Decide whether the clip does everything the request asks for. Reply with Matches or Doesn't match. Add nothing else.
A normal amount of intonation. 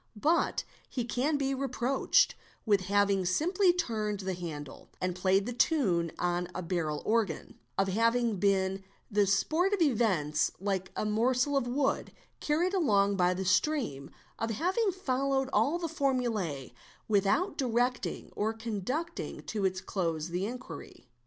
Doesn't match